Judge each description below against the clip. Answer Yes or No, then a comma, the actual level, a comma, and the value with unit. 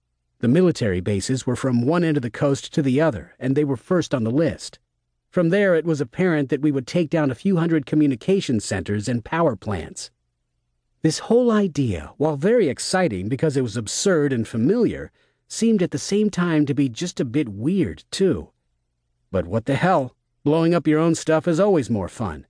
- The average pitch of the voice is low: No, medium, 145 Hz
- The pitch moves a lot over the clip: Yes, wide, 7.0 semitones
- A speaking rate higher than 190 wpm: Yes, average, 200 wpm